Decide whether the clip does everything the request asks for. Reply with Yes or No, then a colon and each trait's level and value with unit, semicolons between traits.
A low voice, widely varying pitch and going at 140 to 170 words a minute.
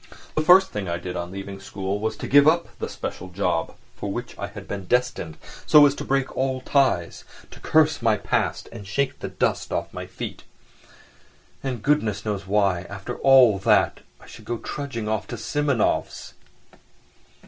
No: low, 110 Hz; wide, 5.8 semitones; average, 180 wpm